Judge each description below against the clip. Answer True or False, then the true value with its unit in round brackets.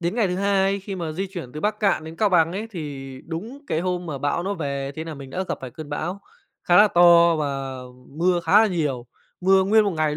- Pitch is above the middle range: False (170 Hz)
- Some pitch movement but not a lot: True (4.4 semitones)